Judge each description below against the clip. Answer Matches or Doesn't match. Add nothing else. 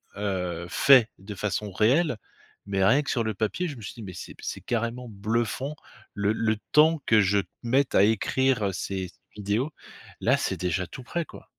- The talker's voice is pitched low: Matches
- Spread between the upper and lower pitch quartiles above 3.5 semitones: Matches